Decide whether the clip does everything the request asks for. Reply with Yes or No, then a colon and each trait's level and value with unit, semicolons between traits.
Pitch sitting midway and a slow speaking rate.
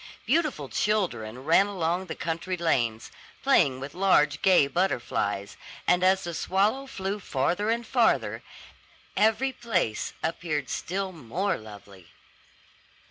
Yes: medium, 175 Hz; slow, 120 wpm